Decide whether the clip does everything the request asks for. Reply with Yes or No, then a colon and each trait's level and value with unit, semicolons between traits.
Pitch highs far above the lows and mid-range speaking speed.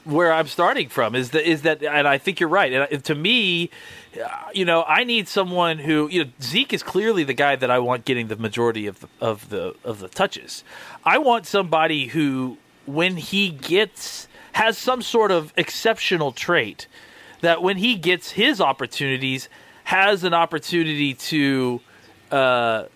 Yes: wide, 6.5 semitones; average, 175 wpm